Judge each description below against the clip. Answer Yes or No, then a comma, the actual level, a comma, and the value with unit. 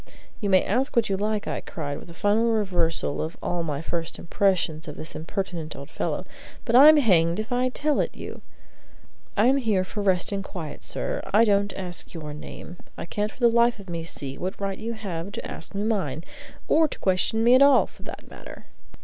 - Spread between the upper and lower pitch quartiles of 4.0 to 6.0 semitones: Yes, average, 5.1 semitones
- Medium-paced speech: No, fast, 215 wpm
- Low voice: No, high, 195 Hz